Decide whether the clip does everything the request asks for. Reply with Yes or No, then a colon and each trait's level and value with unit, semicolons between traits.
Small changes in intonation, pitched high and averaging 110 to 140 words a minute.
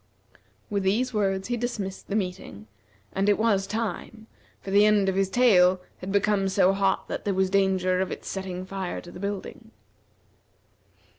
No: narrow, 1.6 semitones; high, 195 Hz; average, 170 wpm